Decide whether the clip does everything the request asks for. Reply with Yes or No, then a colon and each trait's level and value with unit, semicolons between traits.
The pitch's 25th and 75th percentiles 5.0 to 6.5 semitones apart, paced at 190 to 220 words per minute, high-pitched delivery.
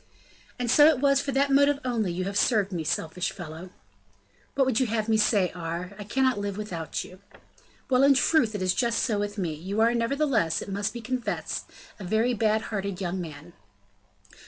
Yes: average, 5.3 semitones; average, 200 wpm; high, 210 Hz